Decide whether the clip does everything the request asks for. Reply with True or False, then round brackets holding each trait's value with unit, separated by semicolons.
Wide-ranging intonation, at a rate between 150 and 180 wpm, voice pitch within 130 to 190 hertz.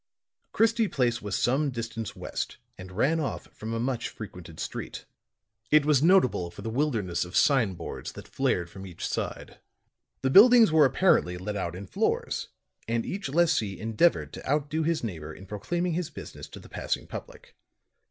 False (8.0 semitones; 170 wpm; 120 Hz)